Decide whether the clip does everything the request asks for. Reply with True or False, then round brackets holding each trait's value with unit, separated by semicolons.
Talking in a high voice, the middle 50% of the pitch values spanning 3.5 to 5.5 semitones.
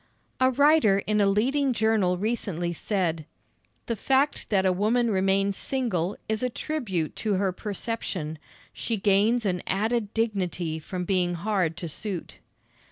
True (200 Hz; 4.0 semitones)